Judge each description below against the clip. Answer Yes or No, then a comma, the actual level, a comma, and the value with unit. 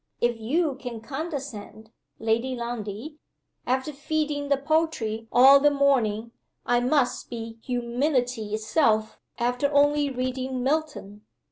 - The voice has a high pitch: Yes, very high, 255 Hz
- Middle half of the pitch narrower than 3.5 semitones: No, average, 4.0 semitones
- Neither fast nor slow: No, slow, 115 wpm